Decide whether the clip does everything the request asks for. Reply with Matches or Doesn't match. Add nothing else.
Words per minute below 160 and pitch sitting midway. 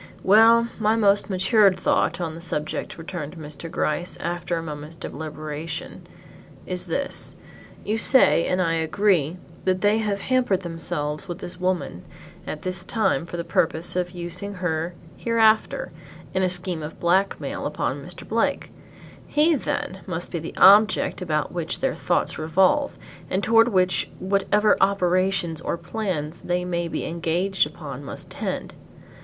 Matches